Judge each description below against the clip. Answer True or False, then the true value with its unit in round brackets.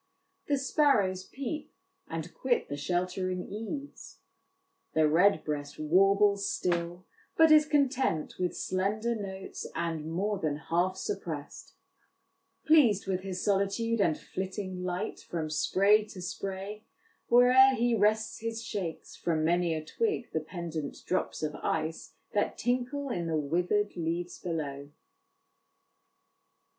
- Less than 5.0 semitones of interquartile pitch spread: False (5.3 semitones)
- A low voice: False (190 Hz)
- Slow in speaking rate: True (125 wpm)